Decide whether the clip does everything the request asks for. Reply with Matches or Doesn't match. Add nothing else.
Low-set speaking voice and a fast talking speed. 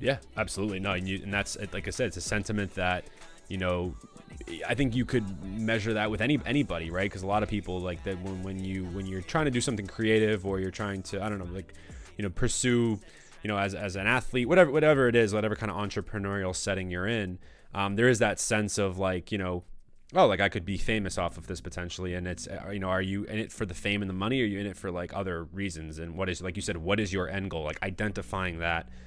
Matches